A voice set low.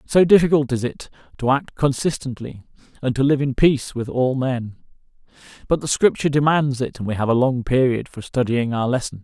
Yes: low, 130 Hz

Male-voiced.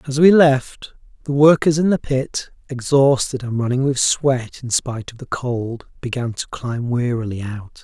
Yes: male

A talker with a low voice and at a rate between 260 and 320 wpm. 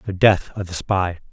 No: very low, 95 Hz; fast, 225 wpm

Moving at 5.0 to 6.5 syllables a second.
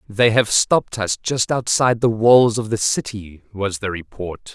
No: 4.5 syllables/s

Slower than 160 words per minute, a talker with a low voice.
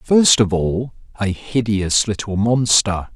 Yes: slow, 135 wpm; low, 105 Hz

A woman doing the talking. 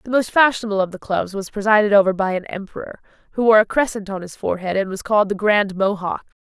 Yes: female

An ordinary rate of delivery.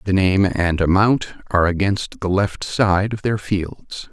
Yes: average, 175 wpm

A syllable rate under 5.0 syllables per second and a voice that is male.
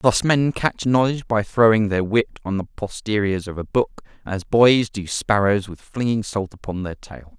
Yes: 4.6 syllables/s; male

